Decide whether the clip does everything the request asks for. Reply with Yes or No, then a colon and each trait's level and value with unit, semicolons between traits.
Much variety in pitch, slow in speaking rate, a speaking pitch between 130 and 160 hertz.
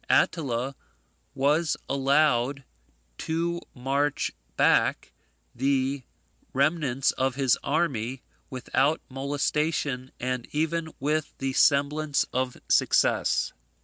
No: average, 2.7 semitones; slow, 85 wpm; medium, 140 Hz